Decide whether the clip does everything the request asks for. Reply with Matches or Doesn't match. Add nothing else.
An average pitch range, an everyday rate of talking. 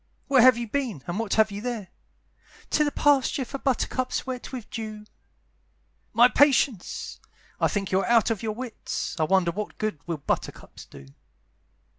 Matches